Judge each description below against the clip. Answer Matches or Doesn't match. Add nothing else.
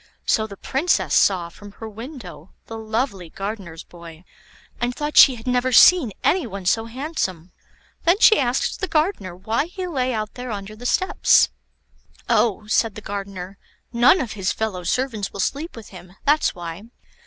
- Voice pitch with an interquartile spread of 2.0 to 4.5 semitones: Doesn't match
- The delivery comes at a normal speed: Matches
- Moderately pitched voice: Doesn't match